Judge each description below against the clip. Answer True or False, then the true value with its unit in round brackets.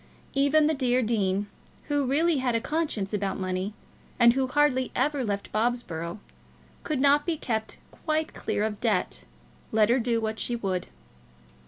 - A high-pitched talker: True (240 Hz)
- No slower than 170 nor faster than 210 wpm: False (160 wpm)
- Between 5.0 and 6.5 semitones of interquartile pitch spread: True (5.3 semitones)